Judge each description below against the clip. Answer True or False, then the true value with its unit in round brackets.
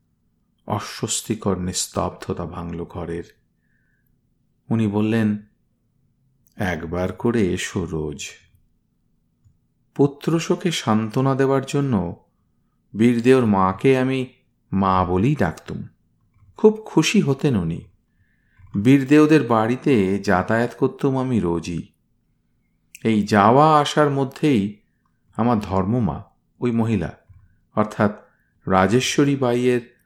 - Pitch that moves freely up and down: True (5.8 semitones)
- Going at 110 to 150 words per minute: False (80 wpm)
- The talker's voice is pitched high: False (115 Hz)